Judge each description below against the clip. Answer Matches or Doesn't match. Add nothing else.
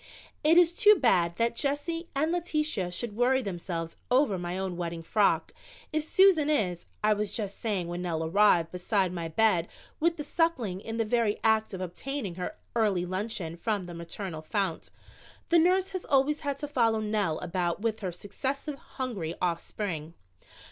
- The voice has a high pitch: Matches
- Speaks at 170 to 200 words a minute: Matches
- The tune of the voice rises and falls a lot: Matches